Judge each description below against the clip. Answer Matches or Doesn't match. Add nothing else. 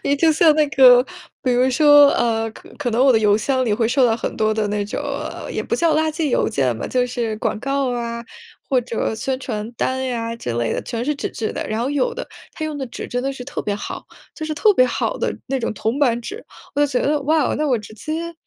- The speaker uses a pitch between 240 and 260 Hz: Matches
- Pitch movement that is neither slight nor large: Matches